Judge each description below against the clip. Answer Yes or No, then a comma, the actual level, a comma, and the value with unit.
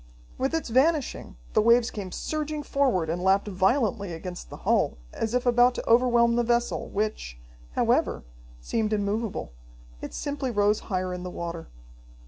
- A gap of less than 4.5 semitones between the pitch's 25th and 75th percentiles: No, average, 4.9 semitones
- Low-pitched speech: No, high, 220 Hz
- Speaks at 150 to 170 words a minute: Yes, average, 155 wpm